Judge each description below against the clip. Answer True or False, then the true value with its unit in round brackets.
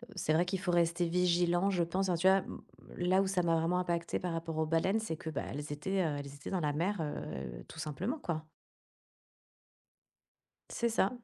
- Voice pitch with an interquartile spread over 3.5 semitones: False (2.9 semitones)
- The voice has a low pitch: False (175 Hz)